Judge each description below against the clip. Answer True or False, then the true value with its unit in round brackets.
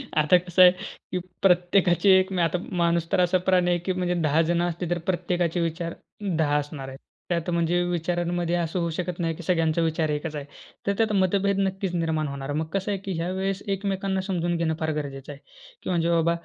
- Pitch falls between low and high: True (175 Hz)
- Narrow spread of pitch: True (2.2 semitones)